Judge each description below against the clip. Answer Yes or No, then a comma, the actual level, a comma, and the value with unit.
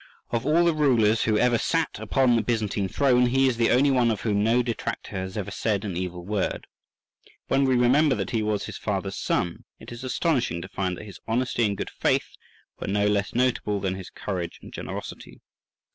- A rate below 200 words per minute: No, fast, 205 wpm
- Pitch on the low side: Yes, low, 115 Hz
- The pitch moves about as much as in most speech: Yes, average, 4.1 semitones